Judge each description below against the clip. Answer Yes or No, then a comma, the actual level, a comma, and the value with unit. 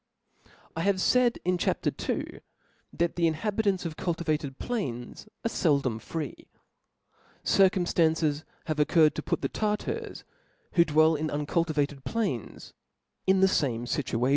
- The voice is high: No, medium, 160 Hz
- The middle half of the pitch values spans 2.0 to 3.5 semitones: No, average, 4.3 semitones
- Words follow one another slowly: Yes, slow, 130 wpm